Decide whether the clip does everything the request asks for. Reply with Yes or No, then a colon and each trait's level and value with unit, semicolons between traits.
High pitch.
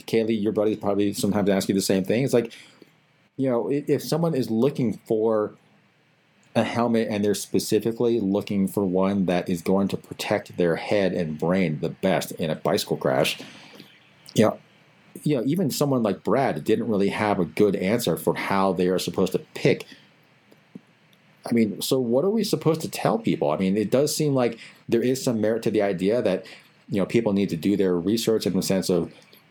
No: low, 105 Hz